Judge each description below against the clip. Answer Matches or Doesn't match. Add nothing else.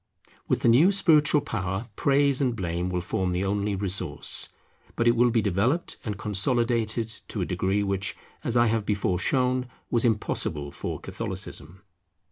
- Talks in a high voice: Doesn't match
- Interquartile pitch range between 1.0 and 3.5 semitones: Doesn't match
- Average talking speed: Matches